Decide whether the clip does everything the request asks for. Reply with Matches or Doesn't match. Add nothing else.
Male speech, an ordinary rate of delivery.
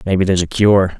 Doesn't match